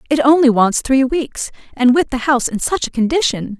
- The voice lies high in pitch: Yes, very high, 260 Hz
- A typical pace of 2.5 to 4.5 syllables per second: No, 5.4 syllables/s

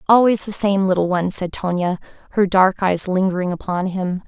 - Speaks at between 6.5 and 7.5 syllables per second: No, 5.4 syllables/s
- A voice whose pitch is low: No, high, 190 Hz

